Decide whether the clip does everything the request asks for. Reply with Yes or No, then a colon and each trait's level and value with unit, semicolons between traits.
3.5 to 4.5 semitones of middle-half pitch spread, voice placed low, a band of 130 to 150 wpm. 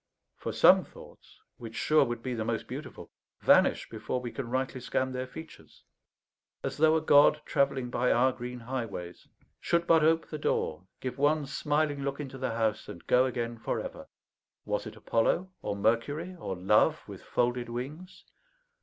No: average, 3.9 semitones; low, 130 Hz; average, 170 wpm